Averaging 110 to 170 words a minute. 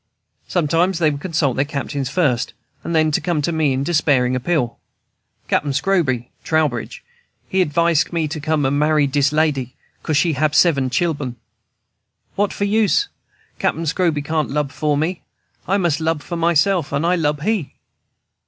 Yes: average, 160 wpm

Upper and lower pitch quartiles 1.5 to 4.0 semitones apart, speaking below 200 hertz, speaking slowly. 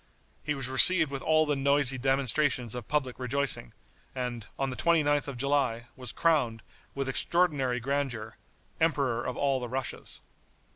No: average, 2.7 semitones; low, 135 Hz; average, 150 wpm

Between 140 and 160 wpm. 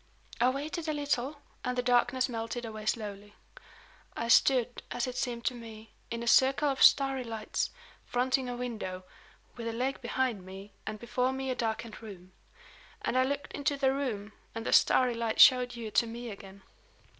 No: average, 180 wpm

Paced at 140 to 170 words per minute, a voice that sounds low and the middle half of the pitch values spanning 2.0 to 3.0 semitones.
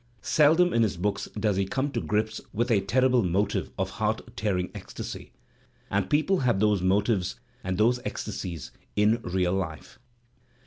No: average, 165 wpm; low, 105 Hz; average, 4.0 semitones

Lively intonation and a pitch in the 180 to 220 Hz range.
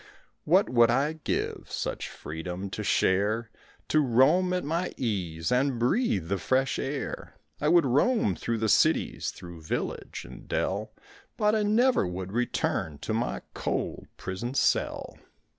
No: wide, 8.3 semitones; low, 120 Hz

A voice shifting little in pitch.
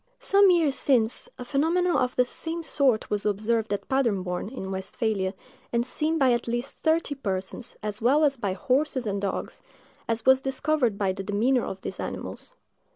No: wide, 5.4 semitones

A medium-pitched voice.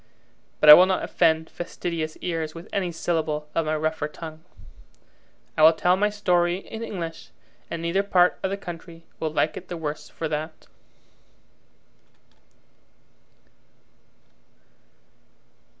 Yes: medium, 165 Hz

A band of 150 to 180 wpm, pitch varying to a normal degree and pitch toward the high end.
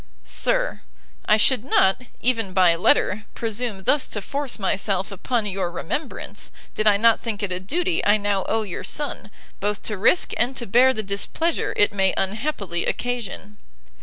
Yes: average, 165 wpm; average, 4.1 semitones; high, 210 Hz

